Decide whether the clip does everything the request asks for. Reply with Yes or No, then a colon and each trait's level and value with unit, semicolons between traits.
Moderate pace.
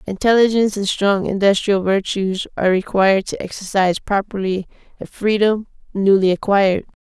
No: slow, 120 wpm